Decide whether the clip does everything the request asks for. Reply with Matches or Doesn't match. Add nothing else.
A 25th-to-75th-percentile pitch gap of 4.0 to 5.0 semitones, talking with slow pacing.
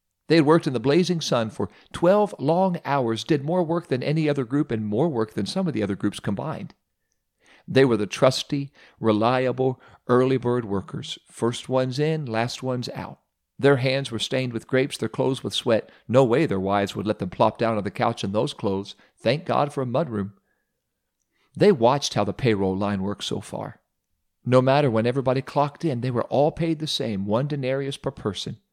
Doesn't match